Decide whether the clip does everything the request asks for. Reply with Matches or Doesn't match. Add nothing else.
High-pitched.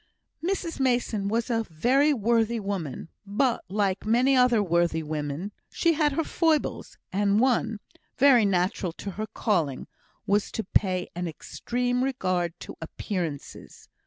Matches